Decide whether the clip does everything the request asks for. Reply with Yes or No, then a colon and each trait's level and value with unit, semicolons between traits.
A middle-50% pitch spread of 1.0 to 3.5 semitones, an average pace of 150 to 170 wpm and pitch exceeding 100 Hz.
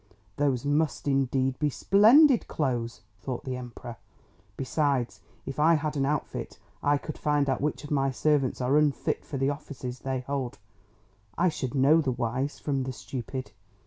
Yes: narrow, 2.5 semitones; average, 165 wpm; low, 135 Hz